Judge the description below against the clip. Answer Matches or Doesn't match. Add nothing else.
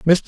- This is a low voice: Doesn't match